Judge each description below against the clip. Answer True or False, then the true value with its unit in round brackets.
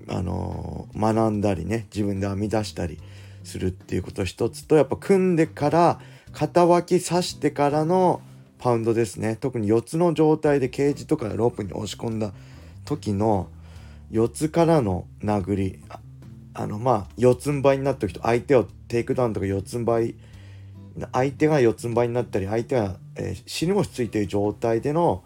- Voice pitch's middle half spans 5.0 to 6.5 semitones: True (5.6 semitones)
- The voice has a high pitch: False (115 Hz)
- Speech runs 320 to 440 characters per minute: True (340 characters per minute)